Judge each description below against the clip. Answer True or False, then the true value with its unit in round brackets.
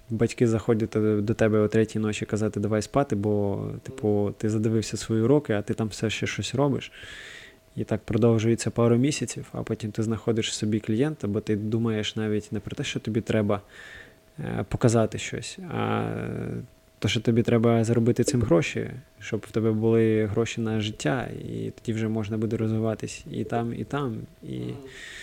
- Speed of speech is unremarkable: False (175 wpm)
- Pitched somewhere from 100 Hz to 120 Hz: True (110 Hz)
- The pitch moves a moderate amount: False (1.5 semitones)